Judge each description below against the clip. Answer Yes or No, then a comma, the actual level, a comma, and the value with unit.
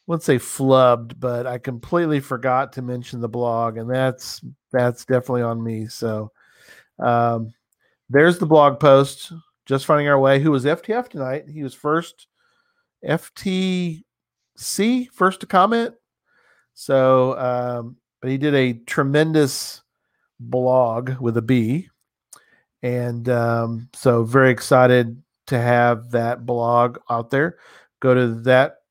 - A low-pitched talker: Yes, low, 130 Hz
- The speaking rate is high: No, slow, 135 wpm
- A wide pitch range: No, average, 3.7 semitones